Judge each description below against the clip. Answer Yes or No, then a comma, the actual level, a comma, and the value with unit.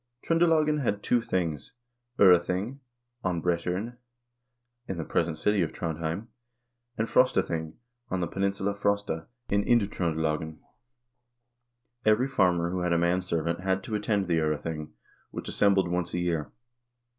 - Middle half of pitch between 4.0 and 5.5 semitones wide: No, average, 3.5 semitones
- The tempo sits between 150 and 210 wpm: No, slow, 135 wpm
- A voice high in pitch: No, very low, 90 Hz